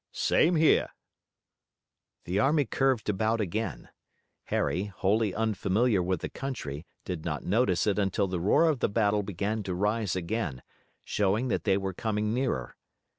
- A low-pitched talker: Yes, low, 105 Hz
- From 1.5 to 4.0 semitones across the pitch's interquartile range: Yes, average, 3.3 semitones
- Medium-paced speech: Yes, average, 150 wpm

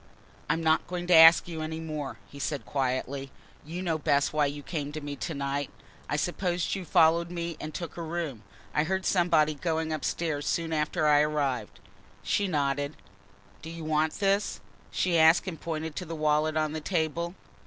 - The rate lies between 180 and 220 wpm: Yes, average, 185 wpm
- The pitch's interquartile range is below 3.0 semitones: Yes, narrow, 2.5 semitones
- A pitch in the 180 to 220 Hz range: No, medium, 155 Hz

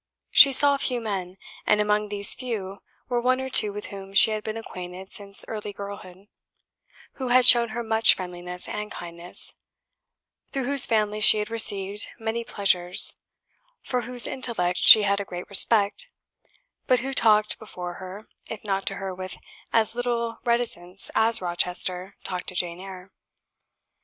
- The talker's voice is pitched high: Yes, high, 210 Hz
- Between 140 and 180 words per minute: Yes, average, 160 wpm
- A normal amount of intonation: Yes, average, 3.7 semitones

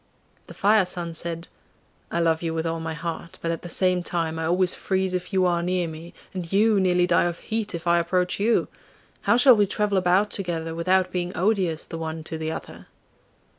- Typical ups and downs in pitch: No, narrow, 2.2 semitones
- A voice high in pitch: No, medium, 175 Hz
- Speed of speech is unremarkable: No, fast, 210 wpm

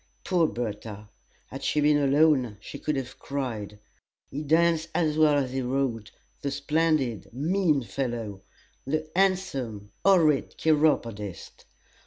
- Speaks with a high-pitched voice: No, medium, 140 Hz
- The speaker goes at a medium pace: No, slow, 125 wpm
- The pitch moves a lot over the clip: No, average, 4.9 semitones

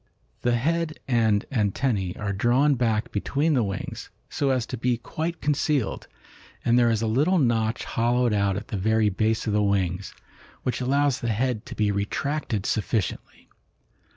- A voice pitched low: Yes, low, 115 Hz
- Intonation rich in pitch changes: No, average, 4.1 semitones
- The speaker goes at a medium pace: Yes, average, 165 wpm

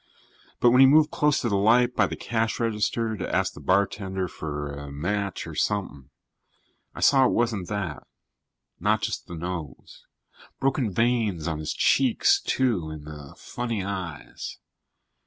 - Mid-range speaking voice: No, low, 100 Hz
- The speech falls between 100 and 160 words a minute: Yes, average, 155 wpm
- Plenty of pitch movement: Yes, wide, 6.3 semitones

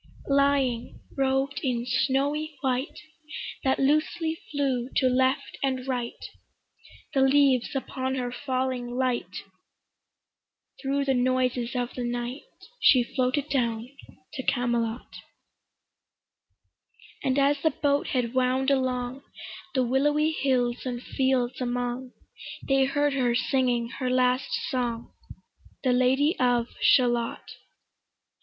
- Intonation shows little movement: Yes, narrow, 1.8 semitones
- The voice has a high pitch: Yes, very high, 260 Hz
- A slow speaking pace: Yes, slow, 110 wpm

